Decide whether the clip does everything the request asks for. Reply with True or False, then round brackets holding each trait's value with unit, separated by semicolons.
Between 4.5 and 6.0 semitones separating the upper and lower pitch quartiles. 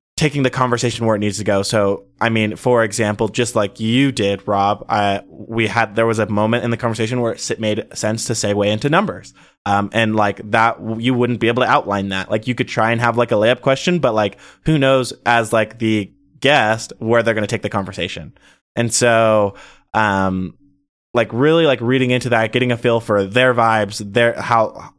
False (2.7 semitones)